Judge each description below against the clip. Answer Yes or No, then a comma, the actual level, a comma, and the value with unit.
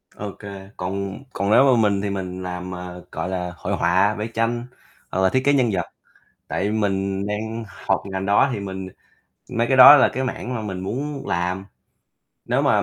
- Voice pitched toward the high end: No, low, 100 Hz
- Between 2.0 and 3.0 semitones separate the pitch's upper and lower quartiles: No, average, 3.4 semitones